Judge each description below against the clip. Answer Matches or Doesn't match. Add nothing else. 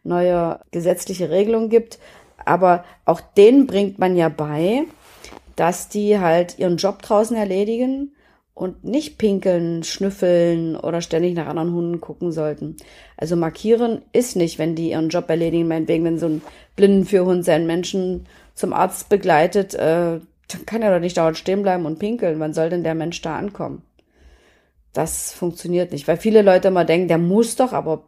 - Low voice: Doesn't match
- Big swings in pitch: Doesn't match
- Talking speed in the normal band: Matches